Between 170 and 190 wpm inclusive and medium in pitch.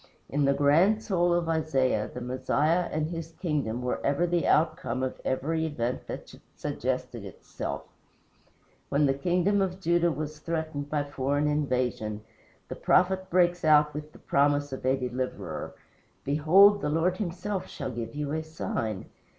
No: average, 155 wpm; medium, 150 Hz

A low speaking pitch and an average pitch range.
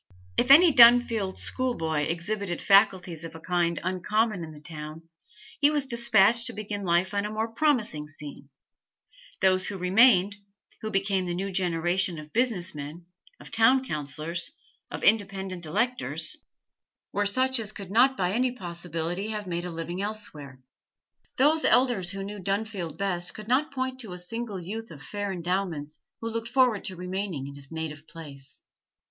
No: high, 190 Hz; average, 4.9 semitones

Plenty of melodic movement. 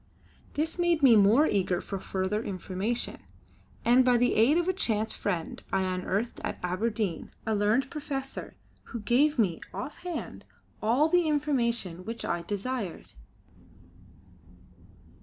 Yes: wide, 5.8 semitones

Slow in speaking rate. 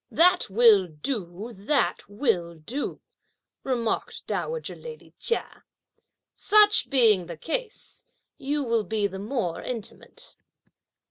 Yes: slow, 110 wpm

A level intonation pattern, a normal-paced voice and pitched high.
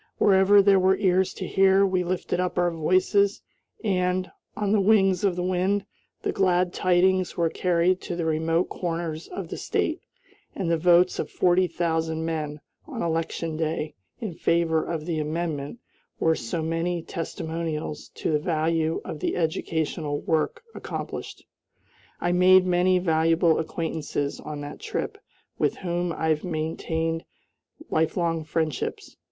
No: narrow, 2.3 semitones; average, 145 wpm; medium, 170 Hz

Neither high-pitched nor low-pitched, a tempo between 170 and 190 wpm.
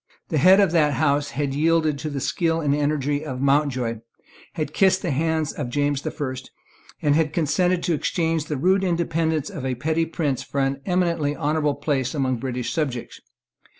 Yes: medium, 150 Hz; average, 185 wpm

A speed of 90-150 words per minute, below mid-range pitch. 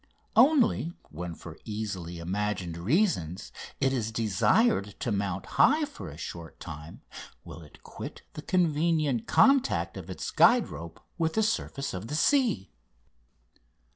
Yes: average, 140 wpm; low, 110 Hz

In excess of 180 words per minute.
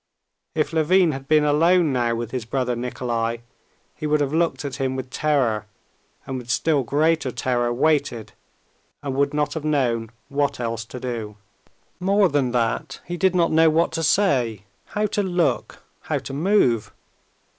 No: average, 165 wpm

